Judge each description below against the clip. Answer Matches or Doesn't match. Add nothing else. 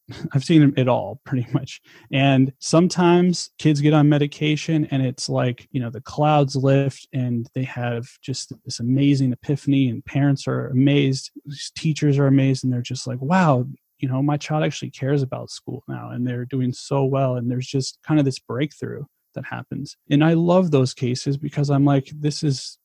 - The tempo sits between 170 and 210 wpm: Matches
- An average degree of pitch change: Doesn't match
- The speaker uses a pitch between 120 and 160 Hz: Matches